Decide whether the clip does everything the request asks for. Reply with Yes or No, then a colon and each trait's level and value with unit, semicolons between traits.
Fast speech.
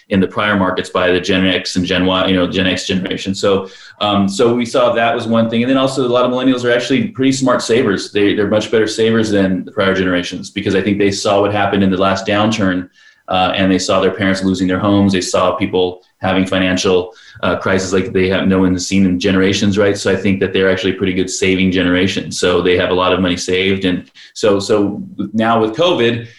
Yes: fast, 240 wpm